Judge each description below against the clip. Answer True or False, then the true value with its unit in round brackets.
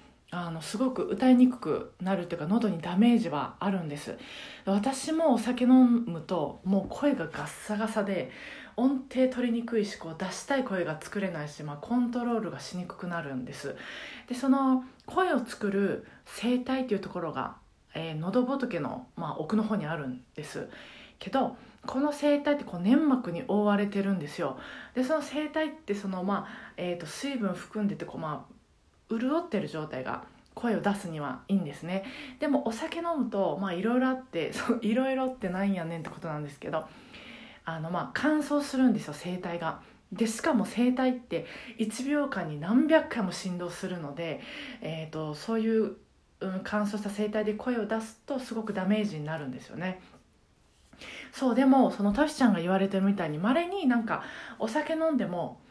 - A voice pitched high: True (215 Hz)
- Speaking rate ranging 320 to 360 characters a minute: True (350 characters per minute)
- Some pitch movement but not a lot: False (6.0 semitones)